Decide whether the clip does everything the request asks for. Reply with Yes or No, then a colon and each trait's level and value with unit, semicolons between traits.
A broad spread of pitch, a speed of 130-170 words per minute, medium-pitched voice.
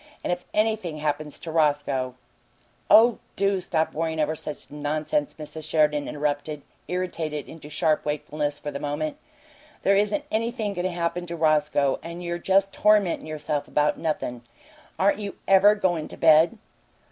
No: average, 4.0 semitones; average, 160 wpm; medium, 160 Hz